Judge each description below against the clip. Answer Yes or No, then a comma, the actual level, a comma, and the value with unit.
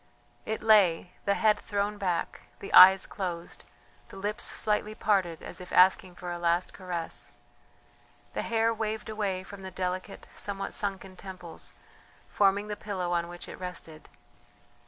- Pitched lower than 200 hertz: Yes, high, 190 Hz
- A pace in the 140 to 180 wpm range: Yes, average, 150 wpm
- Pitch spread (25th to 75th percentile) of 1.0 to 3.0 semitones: Yes, narrow, 2.6 semitones